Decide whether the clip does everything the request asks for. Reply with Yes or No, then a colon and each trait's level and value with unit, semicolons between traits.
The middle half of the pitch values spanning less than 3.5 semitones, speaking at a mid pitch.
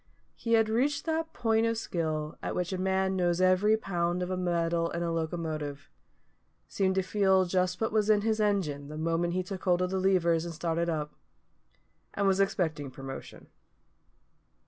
Yes: average, 2.9 semitones; medium, 180 Hz